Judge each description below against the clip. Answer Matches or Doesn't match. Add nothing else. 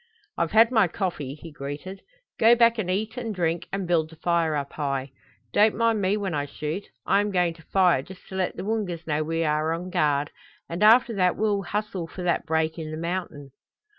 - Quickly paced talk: Matches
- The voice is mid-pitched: Matches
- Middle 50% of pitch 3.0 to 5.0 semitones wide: Matches